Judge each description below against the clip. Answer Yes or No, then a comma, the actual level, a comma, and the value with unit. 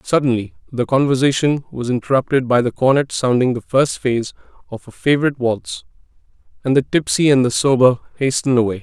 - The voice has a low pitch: Yes, low, 130 Hz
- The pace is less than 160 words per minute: No, average, 165 wpm